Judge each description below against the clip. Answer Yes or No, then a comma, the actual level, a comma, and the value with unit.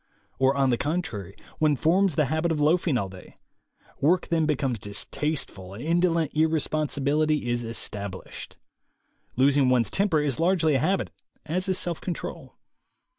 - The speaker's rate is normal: Yes, average, 145 wpm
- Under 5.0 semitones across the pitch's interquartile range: Yes, average, 4.6 semitones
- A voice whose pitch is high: No, medium, 150 Hz